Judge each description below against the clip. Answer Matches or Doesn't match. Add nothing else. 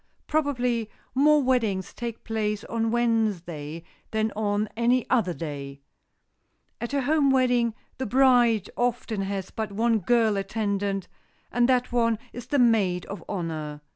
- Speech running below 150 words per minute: Matches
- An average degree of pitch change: Matches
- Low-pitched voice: Doesn't match